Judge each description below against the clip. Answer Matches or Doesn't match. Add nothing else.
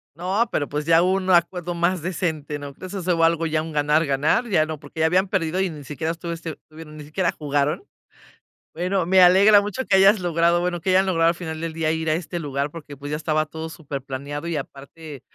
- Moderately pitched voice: Matches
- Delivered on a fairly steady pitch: Doesn't match